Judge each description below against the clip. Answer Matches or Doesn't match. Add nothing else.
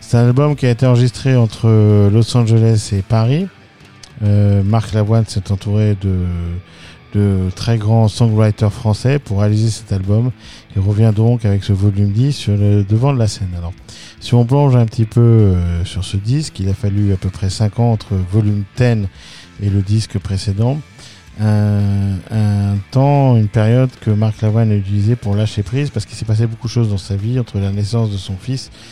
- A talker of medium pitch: Doesn't match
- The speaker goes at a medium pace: Matches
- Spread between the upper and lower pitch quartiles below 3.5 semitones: Matches